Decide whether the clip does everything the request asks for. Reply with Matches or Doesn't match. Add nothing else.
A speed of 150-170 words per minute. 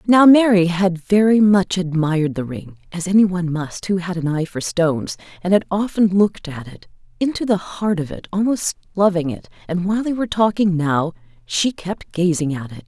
Doesn't match